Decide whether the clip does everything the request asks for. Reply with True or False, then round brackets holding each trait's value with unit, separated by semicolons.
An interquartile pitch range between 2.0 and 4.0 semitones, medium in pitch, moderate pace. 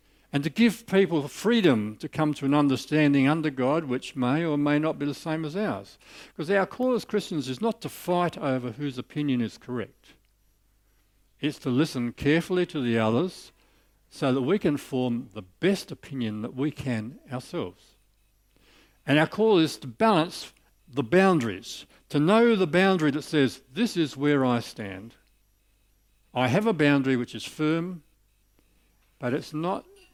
False (5.5 semitones; 145 Hz; 165 wpm)